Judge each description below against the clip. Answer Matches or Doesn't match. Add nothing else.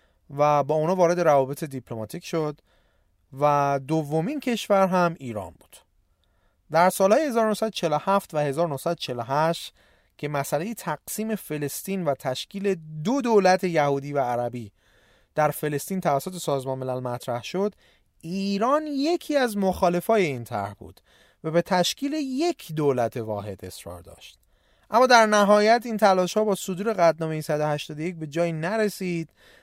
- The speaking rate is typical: Matches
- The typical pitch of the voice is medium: Matches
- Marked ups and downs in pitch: Matches